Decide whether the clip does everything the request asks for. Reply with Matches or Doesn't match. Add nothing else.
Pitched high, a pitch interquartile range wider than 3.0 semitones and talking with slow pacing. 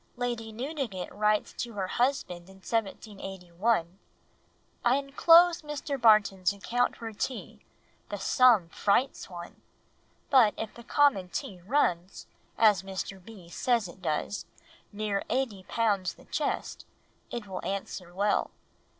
Matches